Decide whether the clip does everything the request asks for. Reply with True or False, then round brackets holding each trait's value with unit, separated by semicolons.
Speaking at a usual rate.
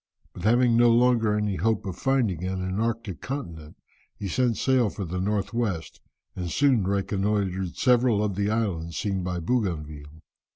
True (160 wpm)